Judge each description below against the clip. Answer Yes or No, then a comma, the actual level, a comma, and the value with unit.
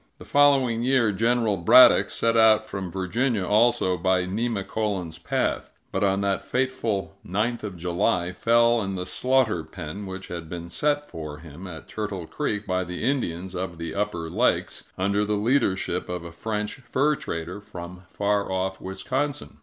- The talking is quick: No, average, 160 wpm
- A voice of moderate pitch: No, low, 100 Hz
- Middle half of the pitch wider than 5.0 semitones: No, average, 4.3 semitones